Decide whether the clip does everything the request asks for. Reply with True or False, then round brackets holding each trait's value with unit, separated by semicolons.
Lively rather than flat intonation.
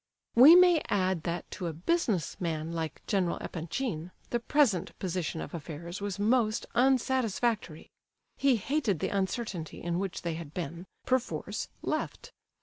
True (6.2 semitones)